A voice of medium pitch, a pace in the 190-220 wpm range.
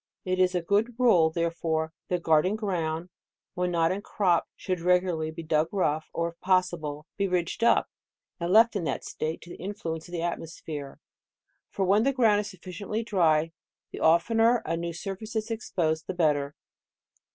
Yes: medium, 175 Hz; average, 195 wpm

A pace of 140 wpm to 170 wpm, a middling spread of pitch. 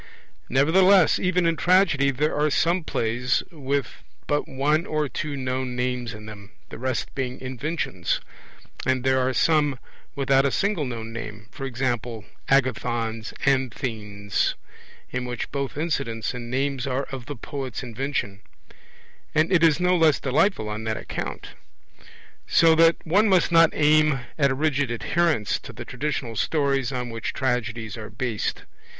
Yes: average, 150 wpm; average, 4.2 semitones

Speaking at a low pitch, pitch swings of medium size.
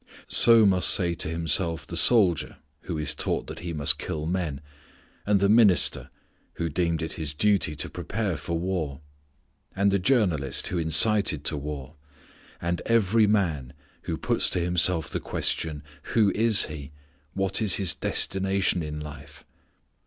Yes: very low, 85 Hz; average, 4.4 semitones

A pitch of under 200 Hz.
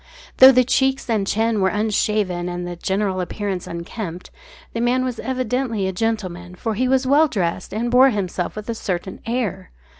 No: high, 215 Hz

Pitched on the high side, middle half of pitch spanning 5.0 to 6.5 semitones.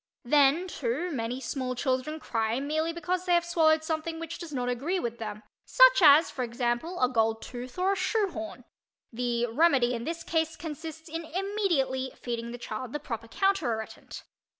Yes: very high, 295 Hz; wide, 5.6 semitones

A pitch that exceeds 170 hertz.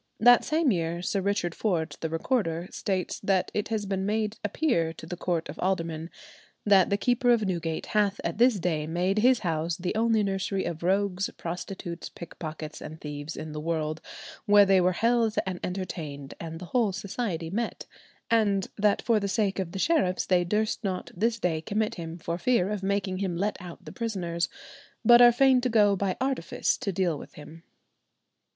Yes: high, 190 Hz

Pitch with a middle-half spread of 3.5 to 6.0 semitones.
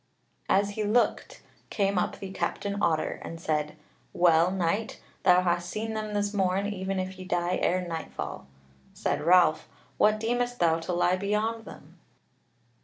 No: average, 3.1 semitones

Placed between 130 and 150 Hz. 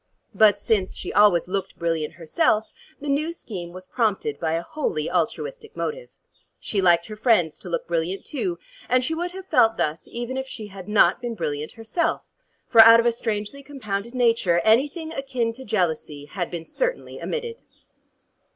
No: high, 220 Hz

